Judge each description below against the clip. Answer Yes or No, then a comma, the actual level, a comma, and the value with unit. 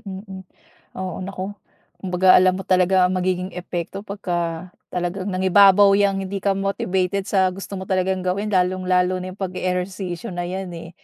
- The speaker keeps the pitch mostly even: Yes, narrow, 1.1 semitones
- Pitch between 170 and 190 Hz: Yes, medium, 185 Hz